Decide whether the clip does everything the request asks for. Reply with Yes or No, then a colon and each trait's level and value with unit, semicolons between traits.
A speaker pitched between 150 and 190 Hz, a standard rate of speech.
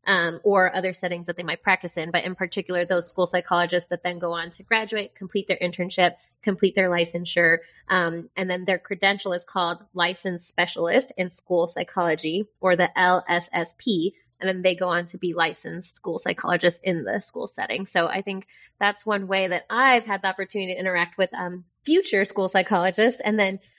Yes: medium, 185 Hz; average, 190 wpm